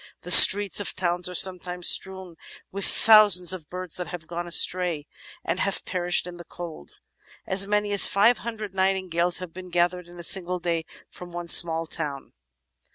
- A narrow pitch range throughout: Yes, narrow, 1.7 semitones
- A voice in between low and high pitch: Yes, medium, 180 Hz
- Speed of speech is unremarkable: Yes, average, 175 wpm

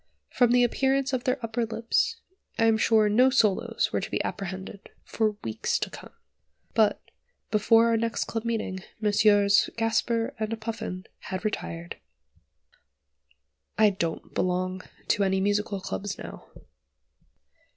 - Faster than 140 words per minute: No, slow, 135 wpm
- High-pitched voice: Yes, high, 215 Hz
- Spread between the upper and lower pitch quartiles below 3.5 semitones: Yes, average, 2.7 semitones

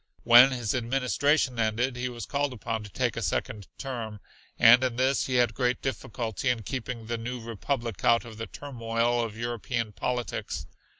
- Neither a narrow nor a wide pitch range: No, narrow, 1.9 semitones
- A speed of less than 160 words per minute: No, average, 175 wpm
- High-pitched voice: No, low, 120 Hz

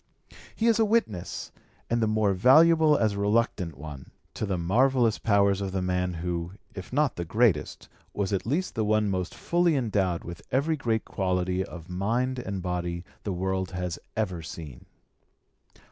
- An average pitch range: Yes, average, 4.9 semitones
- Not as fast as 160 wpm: No, average, 170 wpm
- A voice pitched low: Yes, low, 100 Hz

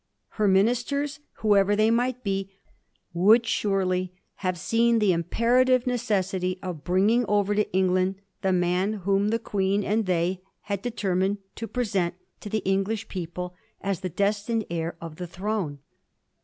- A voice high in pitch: Yes, high, 195 Hz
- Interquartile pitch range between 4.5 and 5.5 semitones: No, average, 3.2 semitones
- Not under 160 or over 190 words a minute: No, average, 145 wpm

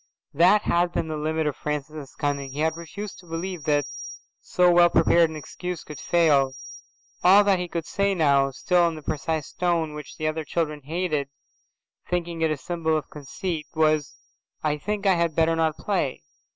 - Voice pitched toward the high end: No, medium, 160 Hz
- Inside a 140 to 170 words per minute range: No, average, 180 wpm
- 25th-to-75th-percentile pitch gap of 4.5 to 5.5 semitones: No, narrow, 2.6 semitones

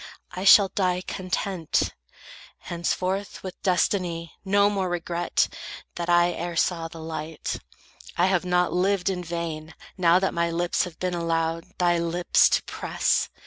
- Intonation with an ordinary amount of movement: No, narrow, 1.6 semitones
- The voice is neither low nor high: Yes, medium, 175 Hz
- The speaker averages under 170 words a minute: Yes, average, 145 wpm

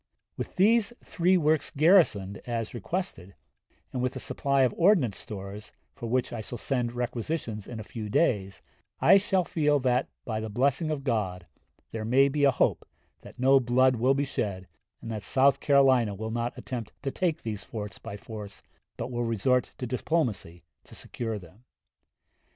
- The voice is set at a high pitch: No, low, 125 Hz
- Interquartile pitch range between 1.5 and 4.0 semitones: No, average, 4.4 semitones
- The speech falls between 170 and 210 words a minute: Yes, average, 175 wpm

